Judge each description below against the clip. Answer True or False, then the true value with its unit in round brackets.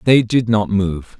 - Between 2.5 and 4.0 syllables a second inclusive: True (3.7 syllables/s)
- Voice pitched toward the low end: True (105 Hz)